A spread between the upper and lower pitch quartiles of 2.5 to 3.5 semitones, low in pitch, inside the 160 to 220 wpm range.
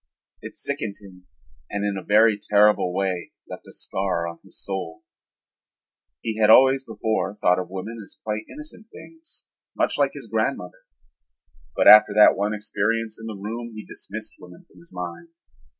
Yes: average, 3.1 semitones; low, 105 Hz; average, 165 wpm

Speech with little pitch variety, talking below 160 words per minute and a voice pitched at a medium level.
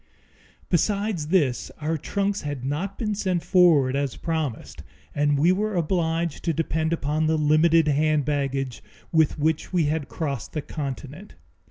No: average, 3.0 semitones; average, 150 wpm; medium, 155 Hz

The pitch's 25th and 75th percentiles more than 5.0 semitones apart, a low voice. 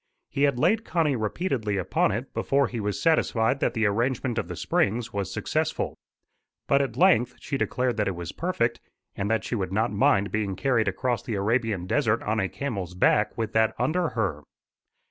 No: average, 4.4 semitones; low, 115 Hz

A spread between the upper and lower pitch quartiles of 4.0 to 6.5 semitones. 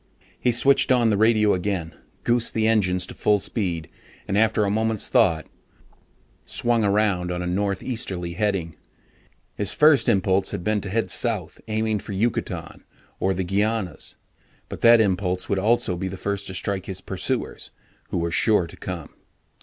No: average, 3.2 semitones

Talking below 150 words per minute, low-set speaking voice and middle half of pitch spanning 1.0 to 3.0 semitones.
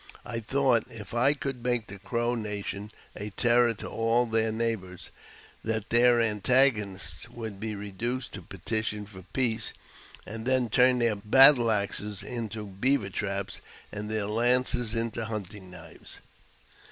Yes: average, 140 wpm; low, 110 Hz; average, 2.7 semitones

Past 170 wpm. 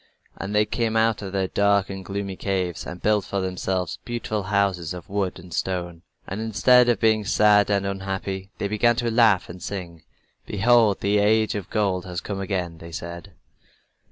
Yes: average, 185 wpm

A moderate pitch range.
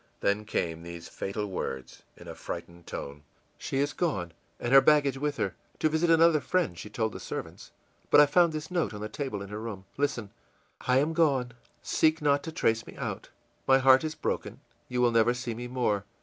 No: wide, 6.2 semitones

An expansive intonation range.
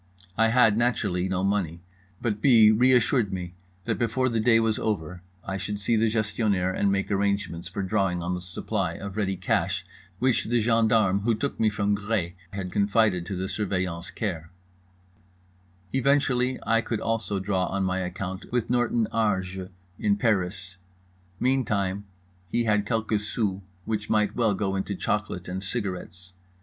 No: average, 3.2 semitones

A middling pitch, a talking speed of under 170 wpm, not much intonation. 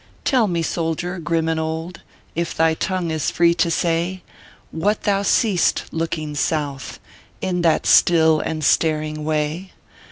Yes: medium, 165 Hz; average, 140 wpm; narrow, 1.8 semitones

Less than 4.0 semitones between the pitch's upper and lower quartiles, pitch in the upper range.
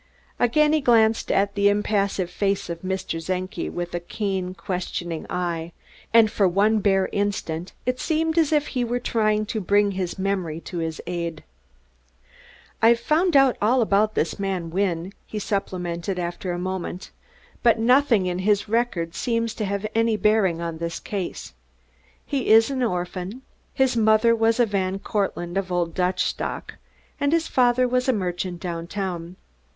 No: average, 4.3 semitones; high, 200 Hz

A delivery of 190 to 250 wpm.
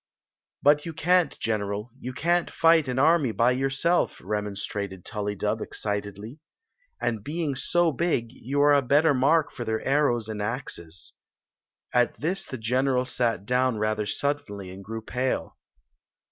No: average, 150 wpm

